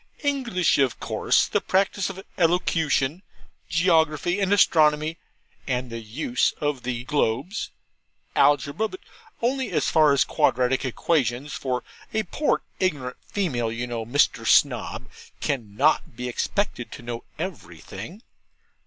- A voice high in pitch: No, medium, 145 Hz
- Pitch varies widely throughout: Yes, wide, 6.5 semitones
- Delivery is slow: Yes, slow, 125 wpm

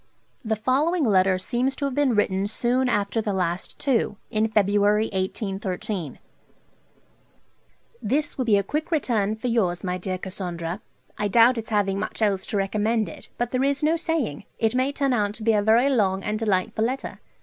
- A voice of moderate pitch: No, high, 215 Hz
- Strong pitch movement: No, average, 4.3 semitones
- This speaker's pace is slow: No, average, 180 wpm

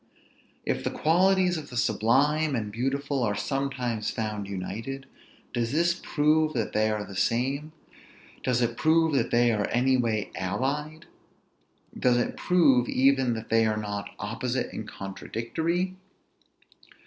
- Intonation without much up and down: No, average, 5.0 semitones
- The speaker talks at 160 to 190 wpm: No, average, 140 wpm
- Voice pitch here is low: Yes, low, 125 Hz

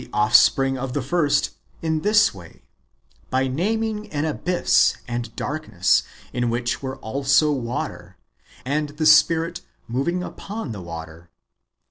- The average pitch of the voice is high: No, medium, 140 Hz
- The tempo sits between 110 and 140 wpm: Yes, slow, 135 wpm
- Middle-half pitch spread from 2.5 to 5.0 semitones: No, wide, 5.4 semitones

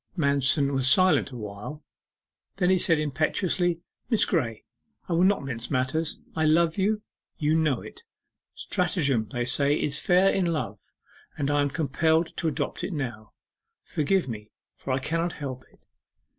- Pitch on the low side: No, medium, 150 Hz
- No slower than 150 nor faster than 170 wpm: Yes, average, 155 wpm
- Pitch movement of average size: Yes, average, 4.3 semitones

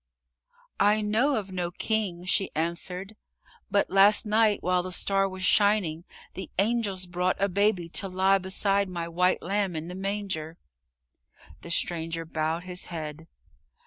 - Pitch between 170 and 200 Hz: Yes, medium, 185 Hz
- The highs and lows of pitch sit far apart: No, average, 2.7 semitones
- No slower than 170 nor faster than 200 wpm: No, average, 145 wpm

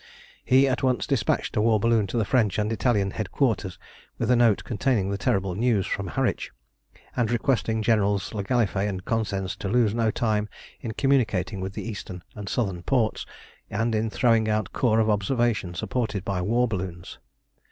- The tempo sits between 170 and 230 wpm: Yes, average, 175 wpm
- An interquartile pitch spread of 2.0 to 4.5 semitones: Yes, average, 3.2 semitones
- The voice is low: Yes, low, 110 Hz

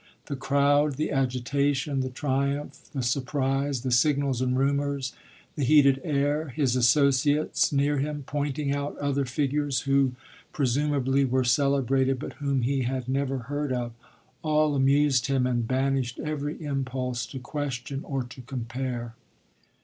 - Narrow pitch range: Yes, narrow, 1.9 semitones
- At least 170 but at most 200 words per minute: No, average, 140 wpm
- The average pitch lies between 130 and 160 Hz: Yes, low, 135 Hz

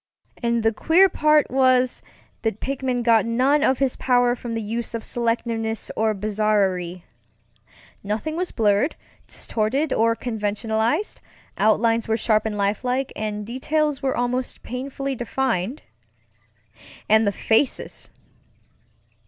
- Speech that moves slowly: Yes, slow, 120 wpm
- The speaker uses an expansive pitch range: No, average, 3.3 semitones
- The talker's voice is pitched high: Yes, high, 235 Hz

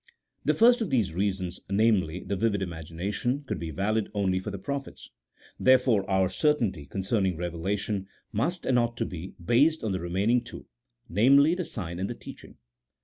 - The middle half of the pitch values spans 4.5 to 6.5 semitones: Yes, average, 4.8 semitones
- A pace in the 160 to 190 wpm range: Yes, average, 175 wpm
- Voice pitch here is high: No, low, 100 Hz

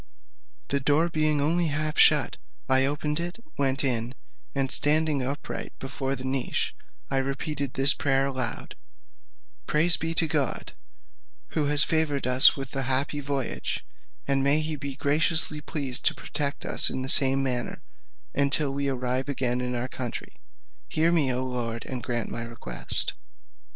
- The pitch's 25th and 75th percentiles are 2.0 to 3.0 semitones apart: Yes, narrow, 2.4 semitones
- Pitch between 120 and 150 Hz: Yes, medium, 140 Hz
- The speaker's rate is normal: Yes, average, 160 wpm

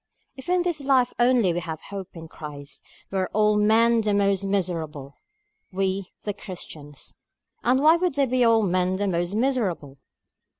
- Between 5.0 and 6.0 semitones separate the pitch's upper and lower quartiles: Yes, wide, 5.6 semitones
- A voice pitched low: No, high, 200 Hz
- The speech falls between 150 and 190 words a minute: Yes, average, 180 wpm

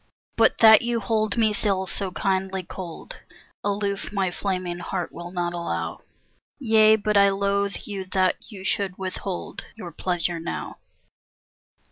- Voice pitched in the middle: No, high, 195 Hz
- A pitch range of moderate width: No, narrow, 2.3 semitones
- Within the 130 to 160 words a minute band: Yes, average, 140 wpm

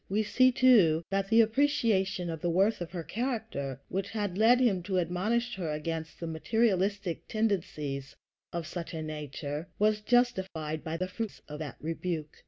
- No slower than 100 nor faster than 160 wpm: No, average, 170 wpm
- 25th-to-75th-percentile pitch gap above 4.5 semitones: Yes, wide, 5.5 semitones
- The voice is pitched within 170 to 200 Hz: Yes, medium, 185 Hz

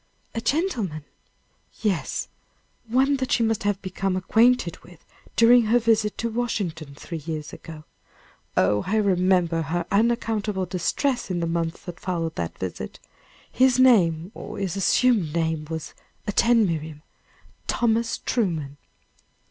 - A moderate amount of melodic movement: No, wide, 5.9 semitones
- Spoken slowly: Yes, slow, 130 wpm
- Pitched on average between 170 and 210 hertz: Yes, high, 190 Hz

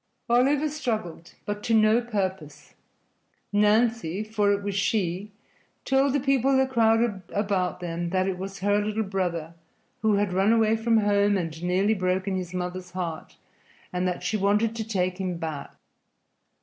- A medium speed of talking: Yes, average, 160 wpm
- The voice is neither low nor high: No, high, 200 Hz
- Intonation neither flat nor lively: Yes, average, 3.3 semitones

